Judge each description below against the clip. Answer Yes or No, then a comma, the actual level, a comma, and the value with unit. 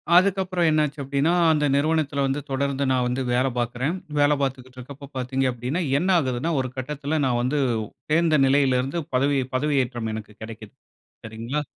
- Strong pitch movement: No, average, 2.9 semitones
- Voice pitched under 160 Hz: Yes, low, 135 Hz